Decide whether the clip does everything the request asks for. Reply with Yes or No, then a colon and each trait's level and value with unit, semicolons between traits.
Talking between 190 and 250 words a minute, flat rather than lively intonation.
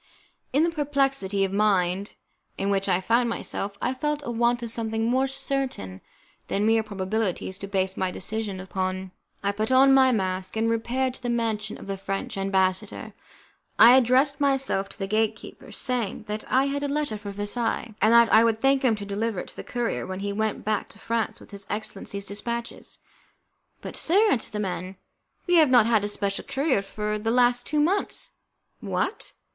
No: average, 195 wpm; average, 4.3 semitones